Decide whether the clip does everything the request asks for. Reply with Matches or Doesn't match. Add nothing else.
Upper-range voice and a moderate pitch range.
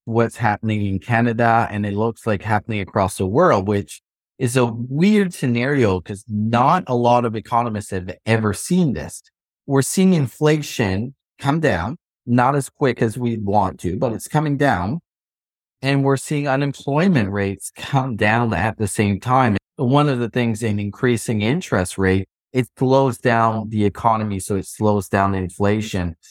Doesn't match